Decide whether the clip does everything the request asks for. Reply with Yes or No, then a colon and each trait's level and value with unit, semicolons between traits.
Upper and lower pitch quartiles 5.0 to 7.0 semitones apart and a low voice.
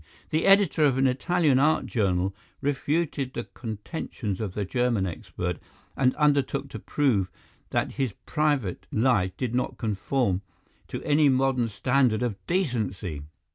Yes: wide, 5.6 semitones; low, 125 Hz